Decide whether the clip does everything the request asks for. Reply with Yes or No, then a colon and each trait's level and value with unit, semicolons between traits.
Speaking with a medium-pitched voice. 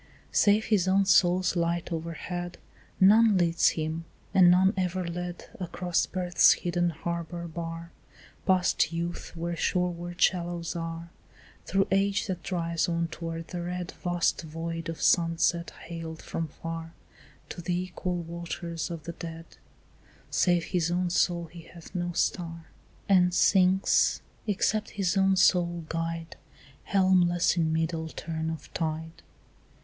Yes: medium, 175 Hz